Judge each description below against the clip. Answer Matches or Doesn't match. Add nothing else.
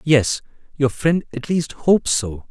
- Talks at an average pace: Matches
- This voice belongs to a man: Matches